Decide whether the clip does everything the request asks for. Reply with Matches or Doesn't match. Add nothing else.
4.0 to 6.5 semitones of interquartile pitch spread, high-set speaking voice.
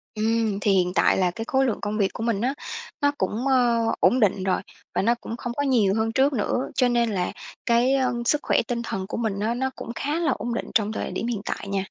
Doesn't match